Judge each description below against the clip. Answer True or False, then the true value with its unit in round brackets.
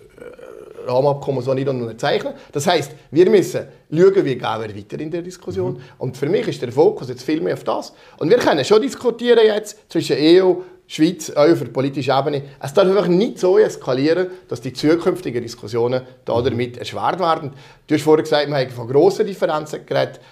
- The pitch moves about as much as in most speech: False (7.9 semitones)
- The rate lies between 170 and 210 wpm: True (185 wpm)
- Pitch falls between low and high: True (165 Hz)